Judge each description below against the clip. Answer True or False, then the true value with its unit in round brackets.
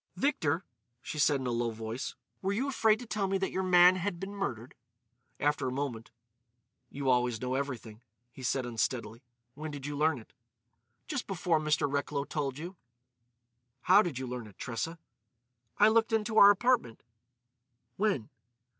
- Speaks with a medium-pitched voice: True (145 Hz)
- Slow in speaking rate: False (165 wpm)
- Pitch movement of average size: False (7.4 semitones)